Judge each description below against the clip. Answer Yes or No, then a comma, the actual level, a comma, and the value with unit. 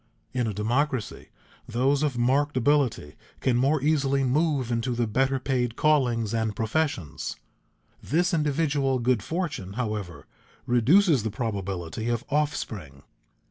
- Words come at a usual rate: No, slow, 125 wpm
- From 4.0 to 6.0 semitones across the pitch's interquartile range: Yes, average, 4.4 semitones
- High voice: No, low, 125 Hz